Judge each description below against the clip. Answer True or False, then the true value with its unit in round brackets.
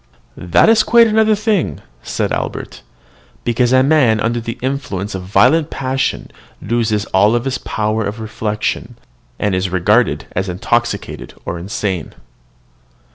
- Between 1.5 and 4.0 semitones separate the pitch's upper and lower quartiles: False (4.7 semitones)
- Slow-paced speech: True (130 wpm)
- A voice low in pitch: True (115 Hz)